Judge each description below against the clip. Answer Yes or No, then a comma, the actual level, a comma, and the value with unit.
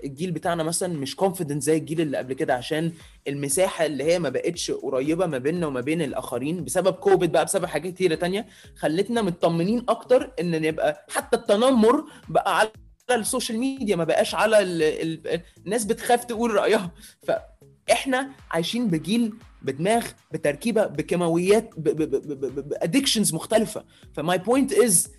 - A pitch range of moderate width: No, wide, 6.2 semitones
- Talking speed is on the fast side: Yes, fast, 160 wpm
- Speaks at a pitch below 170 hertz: No, high, 190 Hz